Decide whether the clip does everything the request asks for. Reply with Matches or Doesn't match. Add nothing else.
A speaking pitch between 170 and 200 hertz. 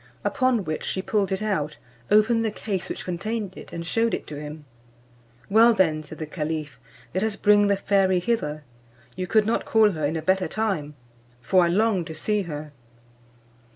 Matches